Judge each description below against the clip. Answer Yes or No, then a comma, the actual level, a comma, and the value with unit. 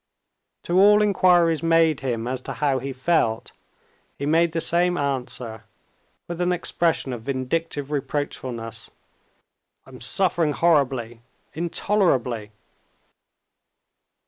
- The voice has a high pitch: No, medium, 145 Hz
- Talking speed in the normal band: No, slow, 105 wpm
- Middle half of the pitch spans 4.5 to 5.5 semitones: Yes, average, 5.1 semitones